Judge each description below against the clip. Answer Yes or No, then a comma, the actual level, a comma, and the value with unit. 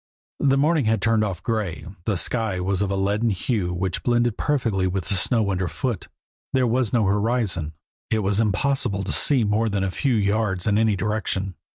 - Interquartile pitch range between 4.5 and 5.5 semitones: No, average, 3.1 semitones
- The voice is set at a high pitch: No, low, 105 Hz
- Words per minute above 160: Yes, average, 190 wpm